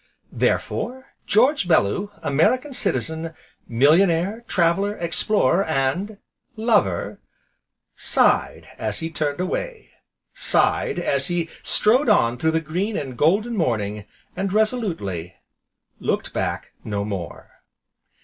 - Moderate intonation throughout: No, wide, 8.0 semitones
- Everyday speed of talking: No, slow, 105 wpm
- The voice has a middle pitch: Yes, medium, 165 Hz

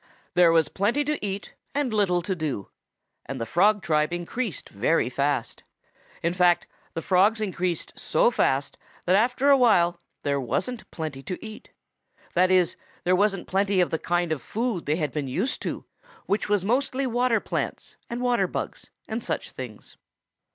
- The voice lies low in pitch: No, medium, 185 Hz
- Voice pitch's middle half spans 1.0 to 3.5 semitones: No, average, 5.3 semitones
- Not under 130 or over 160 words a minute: No, average, 170 wpm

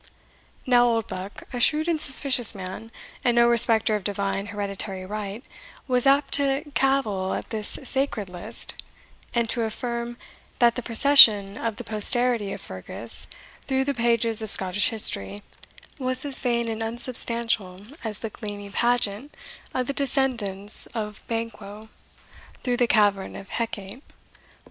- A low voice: No, high, 230 Hz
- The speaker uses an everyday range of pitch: Yes, average, 3.4 semitones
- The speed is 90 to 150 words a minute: Yes, average, 140 wpm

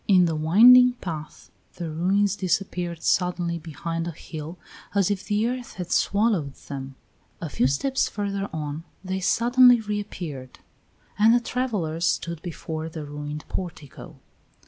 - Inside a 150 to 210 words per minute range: No, average, 140 wpm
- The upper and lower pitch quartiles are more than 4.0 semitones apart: Yes, average, 4.7 semitones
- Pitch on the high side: No, medium, 175 Hz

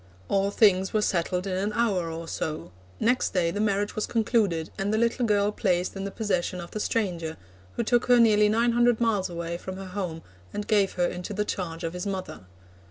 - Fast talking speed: Yes, fast, 215 wpm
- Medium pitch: No, high, 195 Hz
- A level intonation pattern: No, average, 3.3 semitones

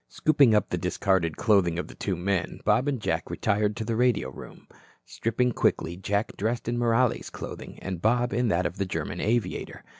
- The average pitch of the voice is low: Yes, low, 105 Hz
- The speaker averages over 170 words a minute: Yes, average, 190 wpm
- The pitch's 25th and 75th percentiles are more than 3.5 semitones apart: Yes, average, 4.8 semitones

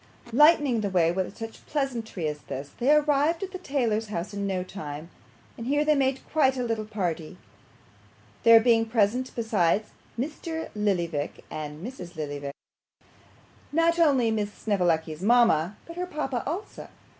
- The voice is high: Yes, high, 225 Hz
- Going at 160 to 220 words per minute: No, average, 150 wpm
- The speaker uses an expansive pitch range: Yes, wide, 7.5 semitones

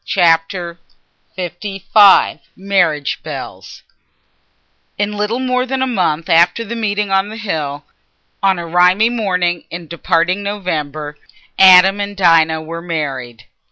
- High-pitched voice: No, medium, 180 Hz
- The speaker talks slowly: Yes, slow, 115 wpm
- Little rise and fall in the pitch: No, average, 3.7 semitones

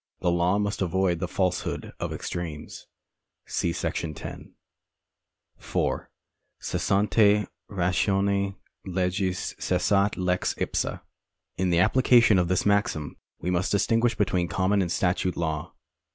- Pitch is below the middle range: Yes, very low, 95 Hz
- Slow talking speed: Yes, slow, 120 wpm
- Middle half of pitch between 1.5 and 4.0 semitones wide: Yes, narrow, 2.4 semitones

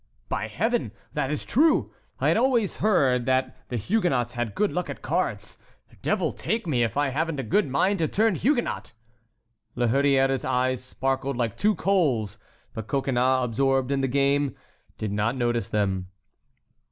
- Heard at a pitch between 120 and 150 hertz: Yes, low, 135 Hz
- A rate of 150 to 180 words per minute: Yes, average, 160 wpm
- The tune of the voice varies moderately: No, wide, 5.9 semitones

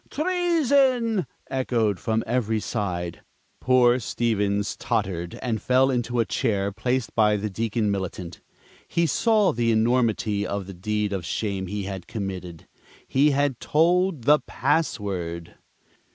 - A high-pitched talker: No, low, 110 Hz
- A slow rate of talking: Yes, slow, 130 wpm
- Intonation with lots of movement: No, average, 4.9 semitones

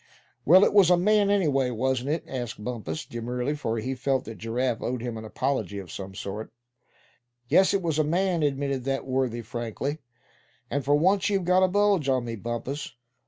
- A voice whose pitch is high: No, low, 135 Hz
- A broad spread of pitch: Yes, wide, 5.9 semitones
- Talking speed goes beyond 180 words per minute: Yes, average, 190 wpm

